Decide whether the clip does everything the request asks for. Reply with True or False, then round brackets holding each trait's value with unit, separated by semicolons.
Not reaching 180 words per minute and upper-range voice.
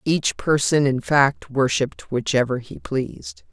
False (135 wpm; 135 Hz)